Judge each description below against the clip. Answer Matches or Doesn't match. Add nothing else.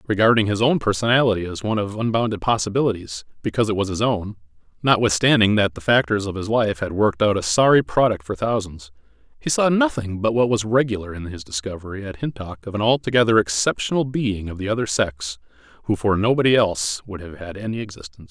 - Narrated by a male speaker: Matches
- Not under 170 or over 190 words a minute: Matches